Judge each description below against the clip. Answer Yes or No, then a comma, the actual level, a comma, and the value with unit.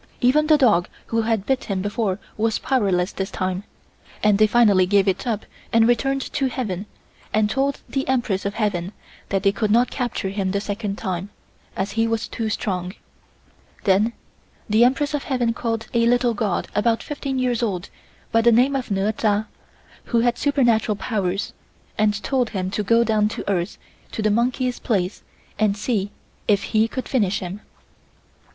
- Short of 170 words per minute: No, average, 175 wpm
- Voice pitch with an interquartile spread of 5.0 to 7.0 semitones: No, average, 3.4 semitones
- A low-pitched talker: No, high, 220 Hz